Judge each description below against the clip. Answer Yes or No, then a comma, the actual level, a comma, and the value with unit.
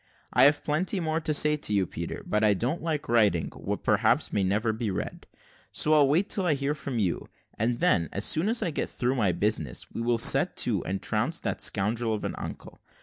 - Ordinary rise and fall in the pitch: No, wide, 6.5 semitones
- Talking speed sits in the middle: No, fast, 225 wpm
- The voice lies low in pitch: Yes, low, 120 Hz